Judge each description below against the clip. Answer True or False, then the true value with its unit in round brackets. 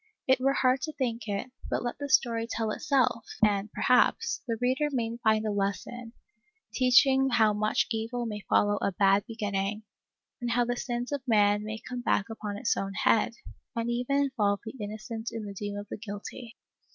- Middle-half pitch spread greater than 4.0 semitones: False (3.0 semitones)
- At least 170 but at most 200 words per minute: True (190 wpm)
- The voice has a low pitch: False (230 Hz)